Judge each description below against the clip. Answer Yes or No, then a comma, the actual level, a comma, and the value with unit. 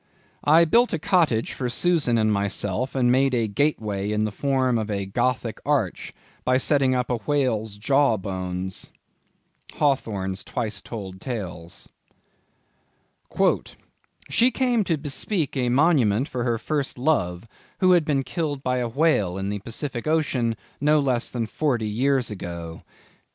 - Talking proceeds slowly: No, average, 145 wpm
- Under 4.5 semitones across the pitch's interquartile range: No, wide, 5.5 semitones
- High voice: No, low, 125 Hz